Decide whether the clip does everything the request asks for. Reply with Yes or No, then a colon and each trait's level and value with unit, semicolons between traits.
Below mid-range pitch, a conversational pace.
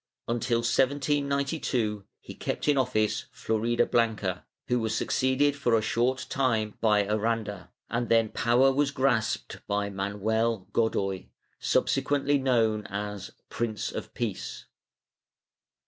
No: low, 115 Hz; slow, 115 wpm